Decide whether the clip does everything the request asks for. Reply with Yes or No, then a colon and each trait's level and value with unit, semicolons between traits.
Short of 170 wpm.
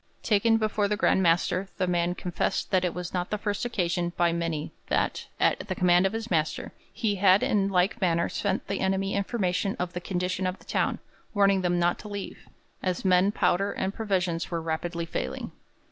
No: average, 195 wpm